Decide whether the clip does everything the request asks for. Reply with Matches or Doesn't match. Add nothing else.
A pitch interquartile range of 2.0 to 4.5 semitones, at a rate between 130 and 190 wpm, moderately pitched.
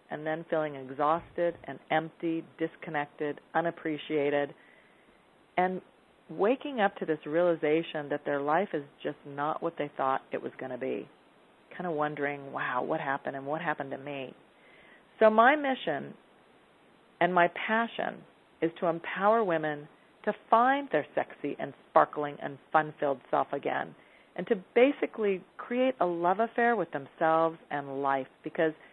Matches